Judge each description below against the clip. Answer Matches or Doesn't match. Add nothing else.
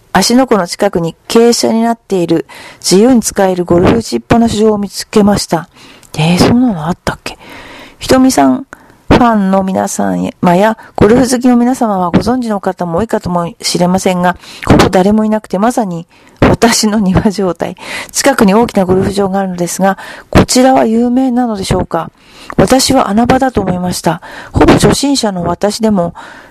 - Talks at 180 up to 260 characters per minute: Doesn't match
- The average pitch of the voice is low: Doesn't match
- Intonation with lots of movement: Doesn't match